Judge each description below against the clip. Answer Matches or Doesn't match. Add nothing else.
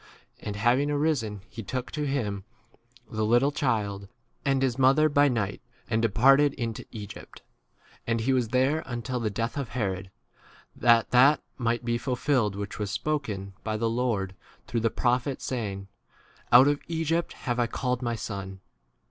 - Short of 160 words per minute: Doesn't match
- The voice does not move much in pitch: Doesn't match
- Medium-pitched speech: Doesn't match